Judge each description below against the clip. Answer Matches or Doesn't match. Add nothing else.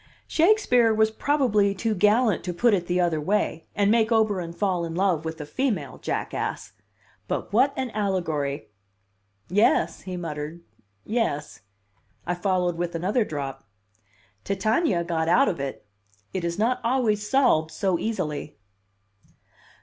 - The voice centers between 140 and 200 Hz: Matches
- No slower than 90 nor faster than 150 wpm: Matches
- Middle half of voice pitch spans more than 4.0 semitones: Matches